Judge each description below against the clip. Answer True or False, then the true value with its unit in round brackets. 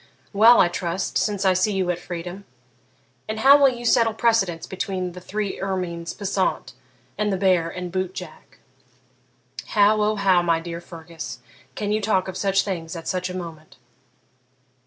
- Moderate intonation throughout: True (3.0 semitones)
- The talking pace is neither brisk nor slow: True (170 wpm)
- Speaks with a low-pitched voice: False (190 Hz)